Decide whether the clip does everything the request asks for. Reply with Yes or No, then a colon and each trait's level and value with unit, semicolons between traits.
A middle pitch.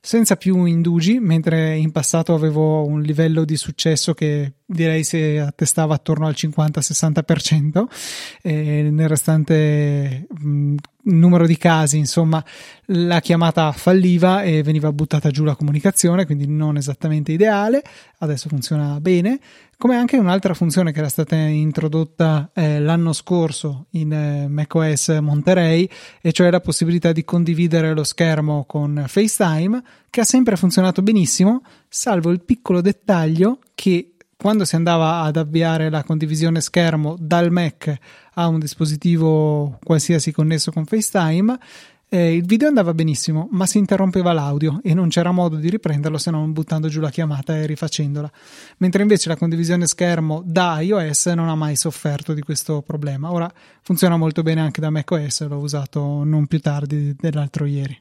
Yes: medium, 160 Hz